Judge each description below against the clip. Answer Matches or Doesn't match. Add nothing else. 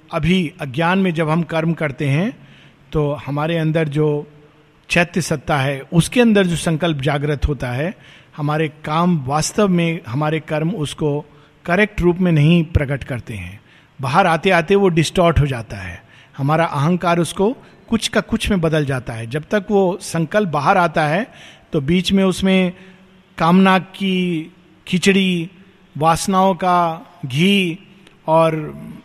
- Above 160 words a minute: Doesn't match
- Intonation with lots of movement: Doesn't match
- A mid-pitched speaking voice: Matches